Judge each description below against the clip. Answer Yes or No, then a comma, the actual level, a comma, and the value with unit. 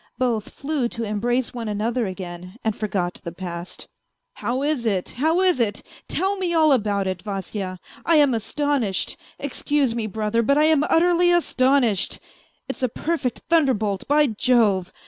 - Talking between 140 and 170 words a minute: Yes, average, 165 wpm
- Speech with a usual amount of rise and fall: No, wide, 6.1 semitones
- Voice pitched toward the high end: Yes, high, 235 Hz